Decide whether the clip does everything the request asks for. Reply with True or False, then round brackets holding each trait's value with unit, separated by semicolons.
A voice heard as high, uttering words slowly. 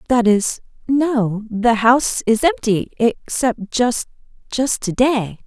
True (230 Hz; 110 wpm)